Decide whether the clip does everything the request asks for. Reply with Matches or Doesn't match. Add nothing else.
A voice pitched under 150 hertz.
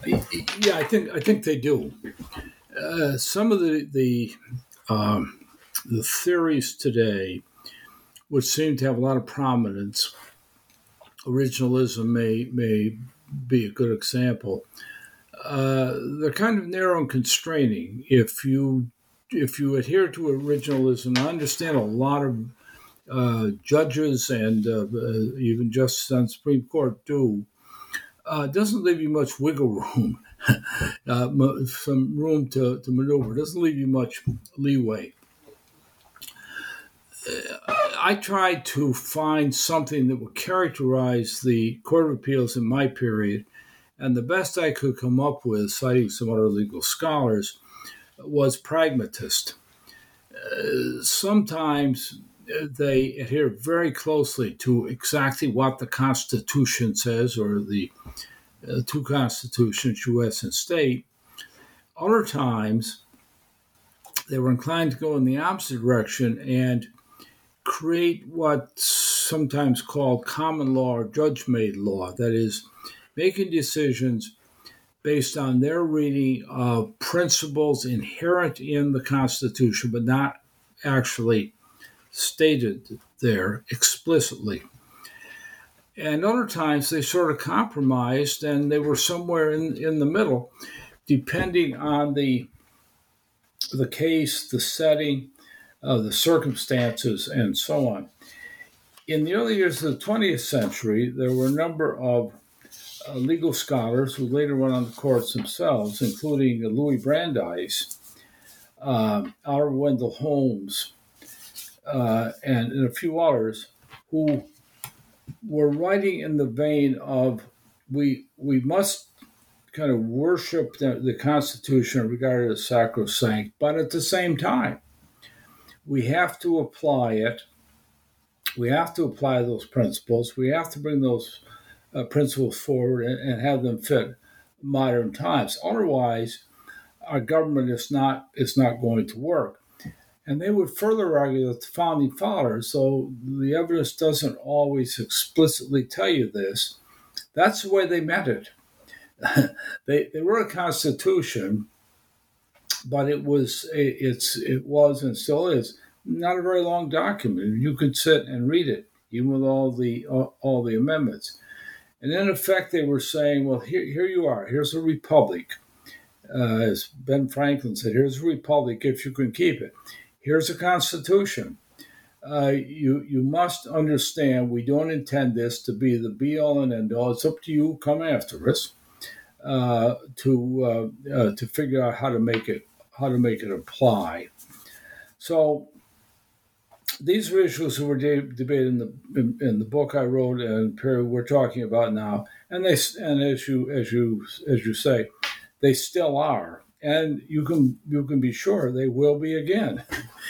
Matches